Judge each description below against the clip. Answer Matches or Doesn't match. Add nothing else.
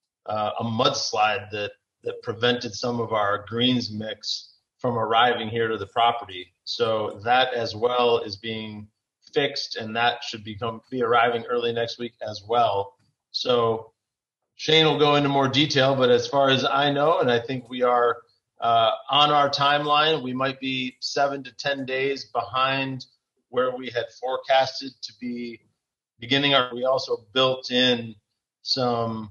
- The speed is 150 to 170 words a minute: Matches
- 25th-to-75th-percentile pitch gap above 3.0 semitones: Doesn't match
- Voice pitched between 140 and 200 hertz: Doesn't match